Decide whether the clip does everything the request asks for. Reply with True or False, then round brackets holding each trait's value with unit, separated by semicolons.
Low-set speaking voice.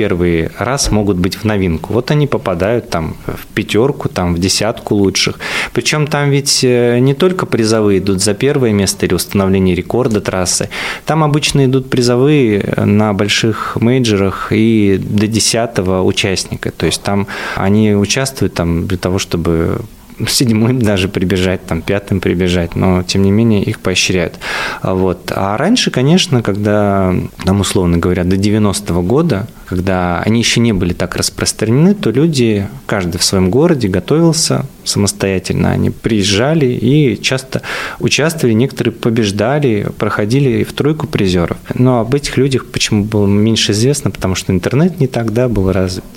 True (105 Hz)